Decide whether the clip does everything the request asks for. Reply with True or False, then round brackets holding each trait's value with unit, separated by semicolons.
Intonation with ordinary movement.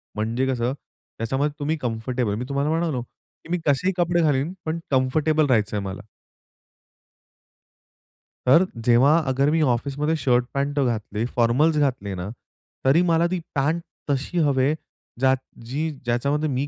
True (4.1 semitones)